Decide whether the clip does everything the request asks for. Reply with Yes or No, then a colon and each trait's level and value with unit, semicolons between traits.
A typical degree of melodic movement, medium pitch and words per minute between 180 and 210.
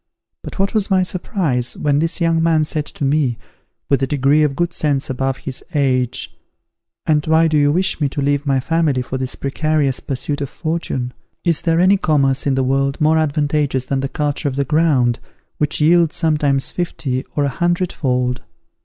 Yes: average, 3.0 semitones; medium, 145 Hz; average, 190 wpm